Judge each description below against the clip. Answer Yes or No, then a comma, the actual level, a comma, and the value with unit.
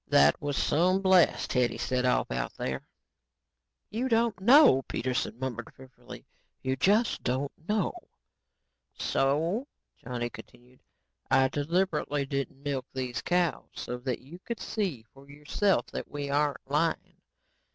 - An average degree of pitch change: No, wide, 6.2 semitones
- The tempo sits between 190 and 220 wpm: No, slow, 135 wpm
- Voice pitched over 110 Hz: Yes, medium, 140 Hz